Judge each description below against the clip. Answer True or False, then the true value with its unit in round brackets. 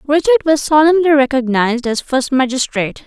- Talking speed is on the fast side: False (135 wpm)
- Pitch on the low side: False (280 Hz)